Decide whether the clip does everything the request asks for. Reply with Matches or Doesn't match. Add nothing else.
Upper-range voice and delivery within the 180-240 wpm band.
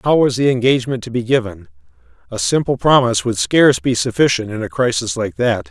Doesn't match